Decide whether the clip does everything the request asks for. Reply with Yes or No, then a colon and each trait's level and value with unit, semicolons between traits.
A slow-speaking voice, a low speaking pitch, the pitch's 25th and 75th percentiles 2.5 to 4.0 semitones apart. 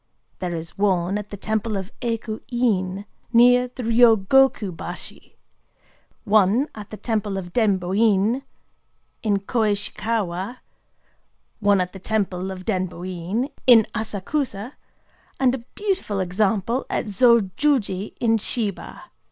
No: slow, 120 wpm; high, 210 Hz; average, 3.5 semitones